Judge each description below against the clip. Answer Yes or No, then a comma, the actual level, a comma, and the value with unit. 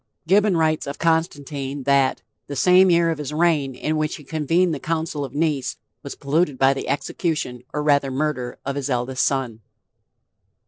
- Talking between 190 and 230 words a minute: No, average, 175 wpm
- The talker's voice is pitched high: No, medium, 150 Hz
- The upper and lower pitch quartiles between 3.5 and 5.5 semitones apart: No, average, 3.0 semitones